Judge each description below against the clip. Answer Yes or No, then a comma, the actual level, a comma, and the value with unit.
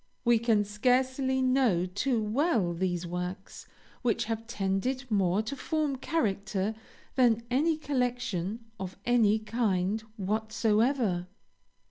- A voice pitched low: No, high, 220 Hz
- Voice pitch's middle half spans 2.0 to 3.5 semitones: No, average, 4.7 semitones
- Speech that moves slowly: Yes, slow, 110 wpm